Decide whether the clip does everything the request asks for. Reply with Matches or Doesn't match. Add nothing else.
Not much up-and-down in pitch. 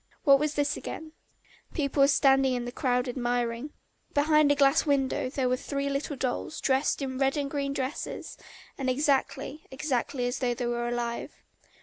Matches